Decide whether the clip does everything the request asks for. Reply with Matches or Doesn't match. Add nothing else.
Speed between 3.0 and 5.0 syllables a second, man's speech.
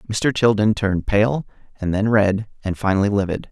Doesn't match